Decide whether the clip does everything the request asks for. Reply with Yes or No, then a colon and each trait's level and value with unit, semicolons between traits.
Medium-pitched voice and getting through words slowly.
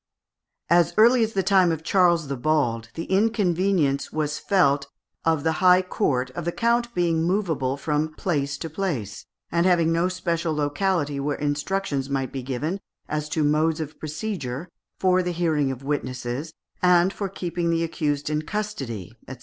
No: medium, 160 Hz; average, 165 wpm